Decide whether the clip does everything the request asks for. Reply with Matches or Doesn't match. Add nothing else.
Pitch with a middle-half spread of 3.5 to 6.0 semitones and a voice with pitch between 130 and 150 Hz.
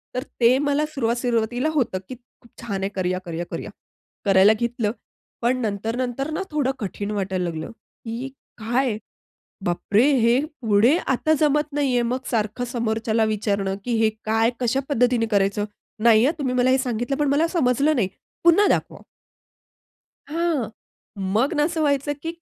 Doesn't match